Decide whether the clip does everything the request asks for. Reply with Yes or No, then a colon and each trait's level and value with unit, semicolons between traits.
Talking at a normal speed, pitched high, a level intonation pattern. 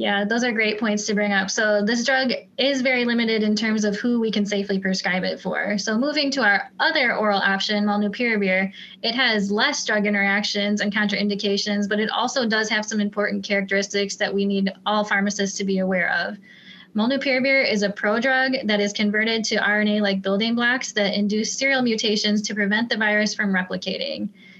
Yes: average, 190 wpm; high, 210 Hz; narrow, 2.0 semitones